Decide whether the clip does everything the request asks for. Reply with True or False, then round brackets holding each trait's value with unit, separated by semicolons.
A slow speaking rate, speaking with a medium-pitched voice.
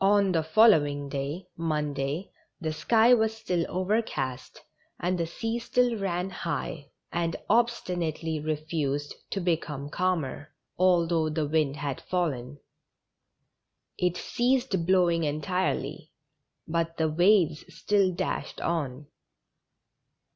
True (110 wpm; 170 Hz)